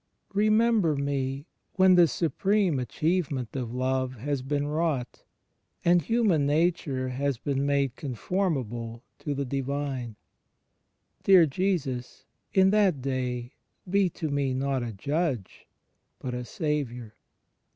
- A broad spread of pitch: No, average, 4.9 semitones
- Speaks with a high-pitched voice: No, medium, 140 Hz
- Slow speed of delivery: Yes, slow, 120 wpm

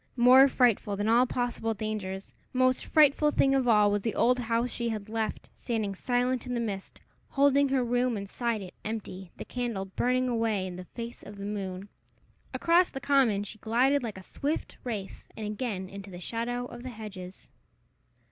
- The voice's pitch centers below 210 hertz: No, high, 230 Hz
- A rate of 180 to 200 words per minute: Yes, average, 185 wpm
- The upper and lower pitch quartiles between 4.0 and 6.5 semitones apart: No, average, 3.5 semitones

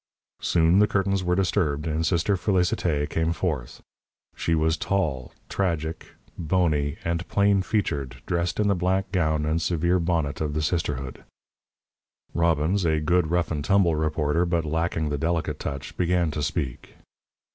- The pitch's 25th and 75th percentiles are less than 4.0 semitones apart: Yes, average, 2.9 semitones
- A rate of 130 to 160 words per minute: Yes, average, 150 wpm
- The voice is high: No, very low, 85 Hz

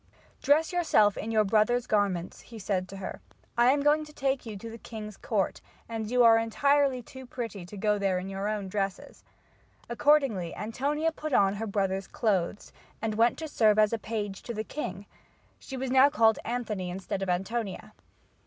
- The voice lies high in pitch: Yes, high, 220 Hz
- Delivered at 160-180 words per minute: No, average, 190 wpm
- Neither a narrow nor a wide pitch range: Yes, average, 4.1 semitones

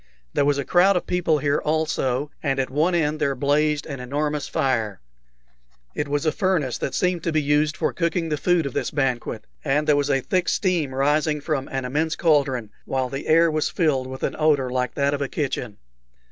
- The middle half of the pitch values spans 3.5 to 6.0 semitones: No, average, 2.8 semitones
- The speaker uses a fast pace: Yes, fast, 210 wpm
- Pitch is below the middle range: No, medium, 145 Hz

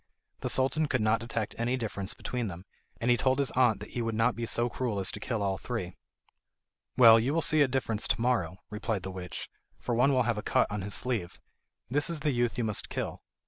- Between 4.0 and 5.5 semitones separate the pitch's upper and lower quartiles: No, average, 3.3 semitones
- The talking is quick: Yes, fast, 235 wpm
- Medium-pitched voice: No, low, 115 Hz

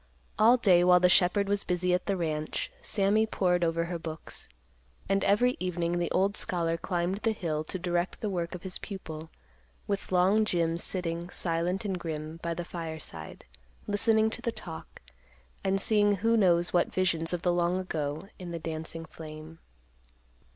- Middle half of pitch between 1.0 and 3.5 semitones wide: Yes, average, 2.9 semitones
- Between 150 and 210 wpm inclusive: Yes, average, 170 wpm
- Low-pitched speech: No, medium, 180 Hz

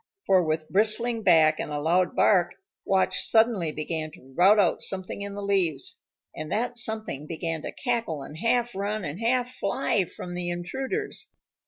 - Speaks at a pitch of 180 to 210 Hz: Yes, high, 190 Hz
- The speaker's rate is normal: Yes, average, 170 wpm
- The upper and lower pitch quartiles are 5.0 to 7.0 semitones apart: Yes, average, 5.3 semitones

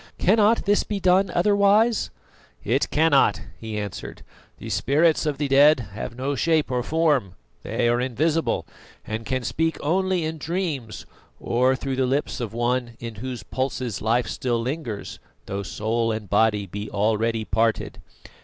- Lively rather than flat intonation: Yes, wide, 6.1 semitones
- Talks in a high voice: No, low, 130 Hz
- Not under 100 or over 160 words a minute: Yes, average, 155 wpm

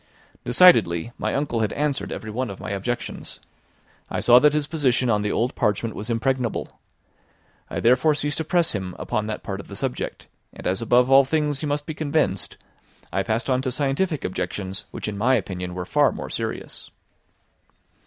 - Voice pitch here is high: No, low, 125 Hz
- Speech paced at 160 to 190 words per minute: Yes, average, 185 wpm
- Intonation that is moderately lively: No, wide, 5.8 semitones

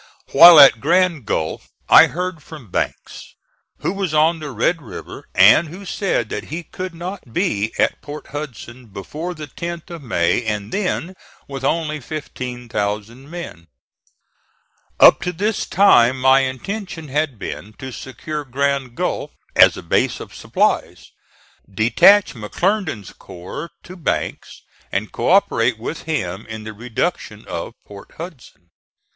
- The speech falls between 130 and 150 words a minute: Yes, average, 140 wpm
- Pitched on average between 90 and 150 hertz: Yes, medium, 140 Hz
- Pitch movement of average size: No, wide, 6.9 semitones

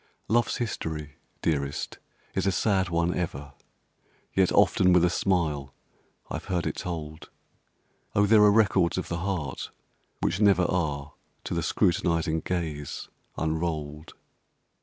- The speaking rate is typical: No, slow, 130 wpm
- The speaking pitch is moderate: No, very low, 85 Hz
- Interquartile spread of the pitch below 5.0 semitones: Yes, average, 3.4 semitones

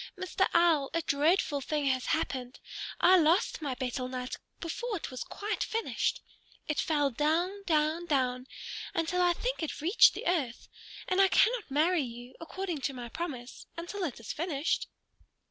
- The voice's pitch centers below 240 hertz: No, very high, 315 Hz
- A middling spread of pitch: Yes, average, 4.9 semitones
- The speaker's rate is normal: Yes, average, 165 wpm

